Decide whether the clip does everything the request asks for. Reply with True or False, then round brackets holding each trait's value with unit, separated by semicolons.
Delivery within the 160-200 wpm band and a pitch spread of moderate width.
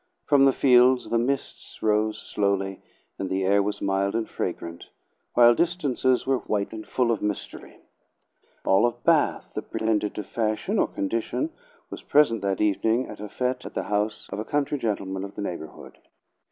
True (175 wpm; 4.2 semitones)